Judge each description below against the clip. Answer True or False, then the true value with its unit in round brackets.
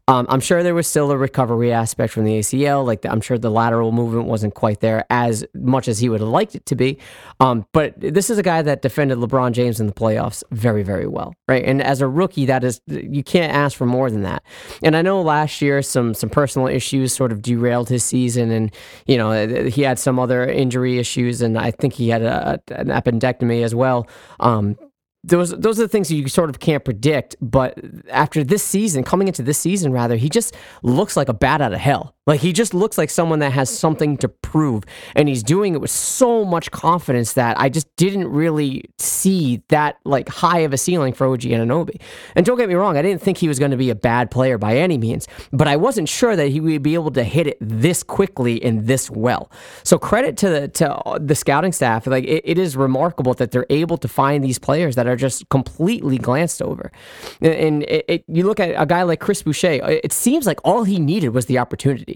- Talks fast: True (235 wpm)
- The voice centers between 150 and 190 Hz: False (135 Hz)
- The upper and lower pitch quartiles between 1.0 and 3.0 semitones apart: False (4.8 semitones)